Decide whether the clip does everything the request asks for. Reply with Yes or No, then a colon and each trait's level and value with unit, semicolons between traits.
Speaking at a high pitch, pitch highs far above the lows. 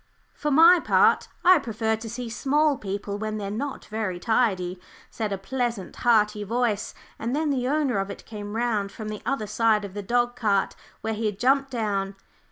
No: high, 220 Hz; average, 3.4 semitones